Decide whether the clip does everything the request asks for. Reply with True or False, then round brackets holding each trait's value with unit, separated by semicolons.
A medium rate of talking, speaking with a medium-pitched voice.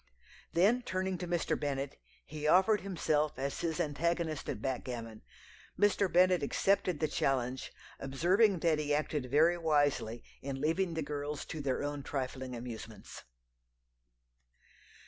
False (130 wpm; 150 Hz)